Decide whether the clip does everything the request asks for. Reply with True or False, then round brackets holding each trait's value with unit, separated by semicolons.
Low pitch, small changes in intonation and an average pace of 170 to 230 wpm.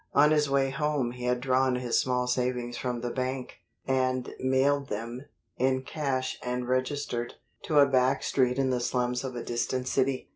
True (130 Hz; 1.4 semitones; 180 wpm)